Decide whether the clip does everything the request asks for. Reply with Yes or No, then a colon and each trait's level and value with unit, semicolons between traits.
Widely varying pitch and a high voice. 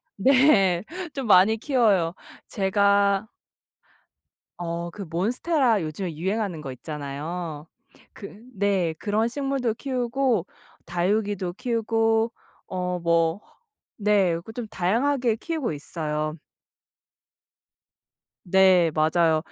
No: average, 4.9 semitones; high, 195 Hz